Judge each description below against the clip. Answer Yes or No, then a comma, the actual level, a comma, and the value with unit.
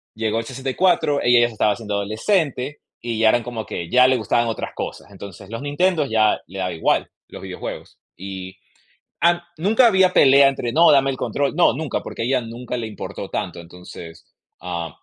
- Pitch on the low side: Yes, low, 120 Hz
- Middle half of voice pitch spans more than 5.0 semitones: Yes, wide, 5.5 semitones